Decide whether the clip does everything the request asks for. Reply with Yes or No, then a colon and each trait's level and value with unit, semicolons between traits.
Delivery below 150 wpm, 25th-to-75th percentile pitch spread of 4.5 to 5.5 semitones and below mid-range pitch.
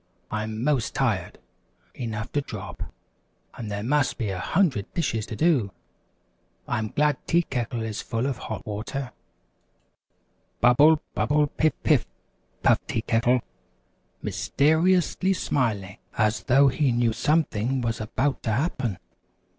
Yes: average, 140 wpm; average, 5.0 semitones; low, 125 Hz